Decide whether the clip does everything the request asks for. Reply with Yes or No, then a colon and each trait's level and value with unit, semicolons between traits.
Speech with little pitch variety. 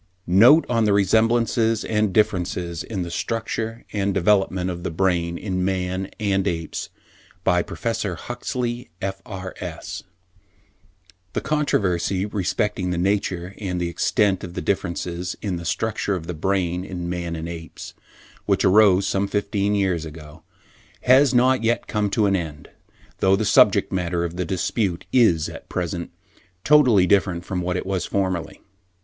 No: average, 3.2 semitones